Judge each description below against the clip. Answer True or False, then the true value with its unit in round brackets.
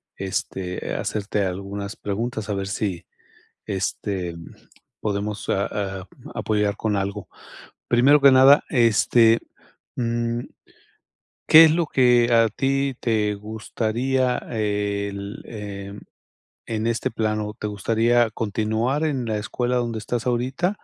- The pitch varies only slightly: False (3.1 semitones)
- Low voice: True (110 Hz)